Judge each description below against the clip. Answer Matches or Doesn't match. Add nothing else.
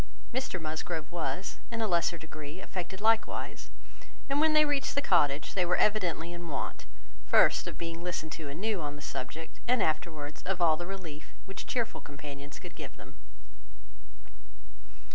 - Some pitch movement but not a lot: Matches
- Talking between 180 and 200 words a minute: Doesn't match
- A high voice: Doesn't match